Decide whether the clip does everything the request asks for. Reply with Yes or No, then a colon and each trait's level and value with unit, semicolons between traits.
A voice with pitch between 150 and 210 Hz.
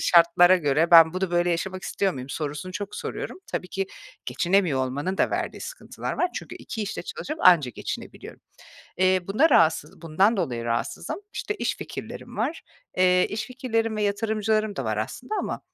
Yes: medium, 185 Hz